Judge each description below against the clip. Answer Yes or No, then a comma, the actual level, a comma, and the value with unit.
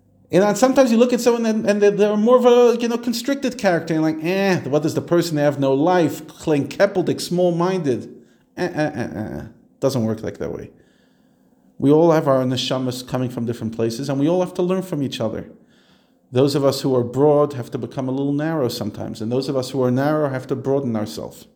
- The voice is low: No, medium, 145 Hz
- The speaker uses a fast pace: Yes, fast, 230 wpm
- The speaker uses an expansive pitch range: Yes, wide, 6.1 semitones